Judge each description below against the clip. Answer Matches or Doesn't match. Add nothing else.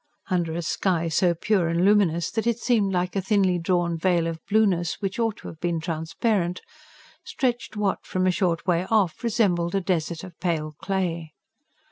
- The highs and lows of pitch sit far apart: Doesn't match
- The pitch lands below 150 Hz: Doesn't match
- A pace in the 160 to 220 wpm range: Matches